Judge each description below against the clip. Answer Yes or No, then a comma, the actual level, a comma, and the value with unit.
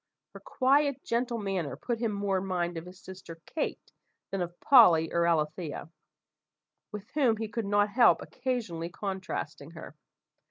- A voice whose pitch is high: Yes, high, 195 Hz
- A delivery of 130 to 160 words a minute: Yes, average, 155 wpm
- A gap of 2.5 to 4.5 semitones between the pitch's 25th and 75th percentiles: No, wide, 5.4 semitones